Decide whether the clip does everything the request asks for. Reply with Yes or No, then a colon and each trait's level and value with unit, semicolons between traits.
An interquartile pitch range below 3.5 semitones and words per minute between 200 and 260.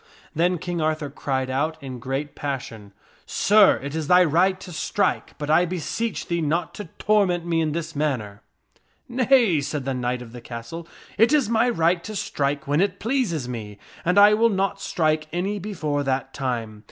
No: wide, 5.5 semitones; fast, 205 wpm